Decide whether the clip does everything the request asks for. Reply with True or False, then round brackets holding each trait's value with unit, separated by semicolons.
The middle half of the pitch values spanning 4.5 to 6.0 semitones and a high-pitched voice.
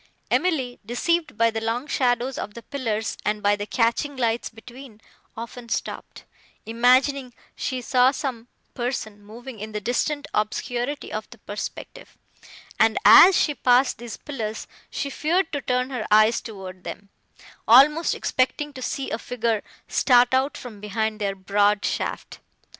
False (3.5 semitones; 240 Hz)